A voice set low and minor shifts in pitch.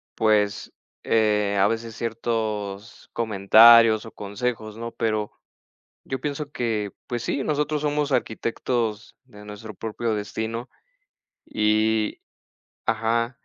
Yes: low, 110 Hz; narrow, 1.8 semitones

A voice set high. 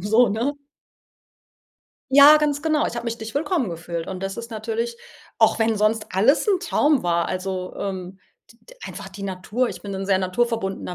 Yes: high, 220 Hz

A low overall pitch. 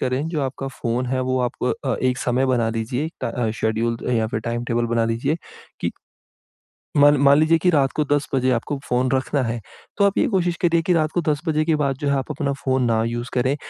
Yes: low, 130 Hz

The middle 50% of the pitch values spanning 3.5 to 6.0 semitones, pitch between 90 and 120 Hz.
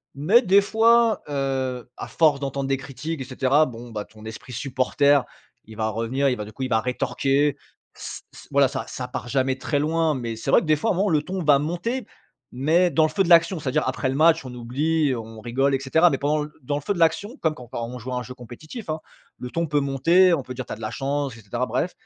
No: average, 4.2 semitones; medium, 140 Hz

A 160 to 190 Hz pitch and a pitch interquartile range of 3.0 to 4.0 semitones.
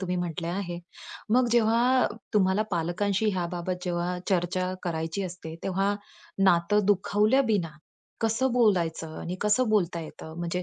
Yes: medium, 185 Hz; average, 3.3 semitones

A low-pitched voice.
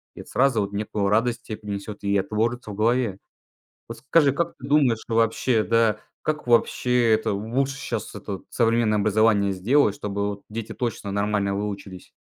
Yes: low, 110 Hz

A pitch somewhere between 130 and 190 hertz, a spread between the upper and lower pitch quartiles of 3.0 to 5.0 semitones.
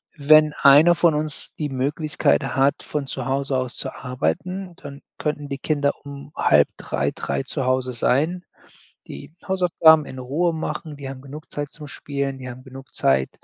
No: medium, 140 Hz; narrow, 2.5 semitones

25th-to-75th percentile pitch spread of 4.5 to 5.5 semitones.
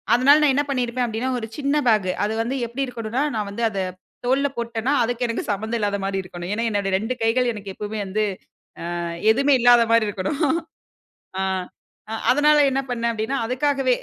No: average, 3.5 semitones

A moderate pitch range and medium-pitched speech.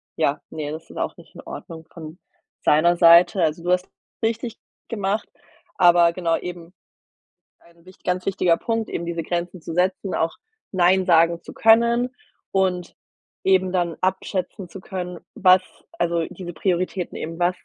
No: narrow, 1.9 semitones; medium, 180 Hz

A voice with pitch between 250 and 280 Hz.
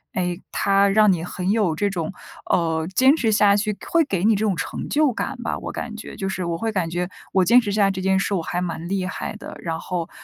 No: high, 195 Hz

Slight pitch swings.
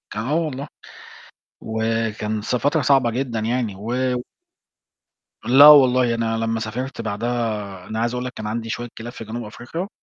Yes: narrow, 2.3 semitones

